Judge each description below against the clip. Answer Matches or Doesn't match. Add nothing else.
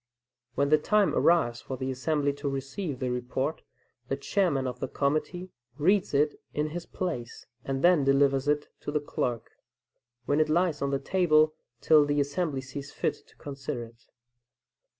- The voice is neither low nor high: Matches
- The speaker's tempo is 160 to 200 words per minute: Matches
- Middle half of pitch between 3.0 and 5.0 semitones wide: Doesn't match